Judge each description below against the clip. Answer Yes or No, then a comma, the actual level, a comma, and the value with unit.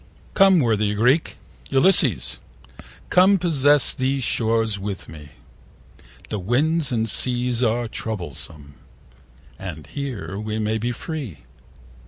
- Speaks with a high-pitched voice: No, low, 115 Hz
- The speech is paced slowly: Yes, slow, 110 wpm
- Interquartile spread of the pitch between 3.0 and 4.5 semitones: No, average, 5.0 semitones